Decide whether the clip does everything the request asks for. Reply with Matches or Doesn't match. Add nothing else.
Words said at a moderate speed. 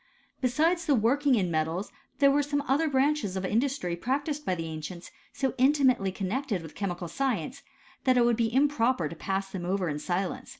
Matches